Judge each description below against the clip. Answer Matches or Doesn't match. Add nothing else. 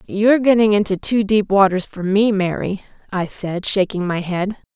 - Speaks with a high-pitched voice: Matches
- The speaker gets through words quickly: Doesn't match